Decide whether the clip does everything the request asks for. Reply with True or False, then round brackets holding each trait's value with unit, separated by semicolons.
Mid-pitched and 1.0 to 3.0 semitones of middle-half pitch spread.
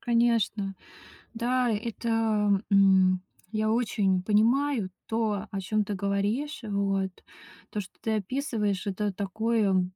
False (210 Hz; 2.7 semitones)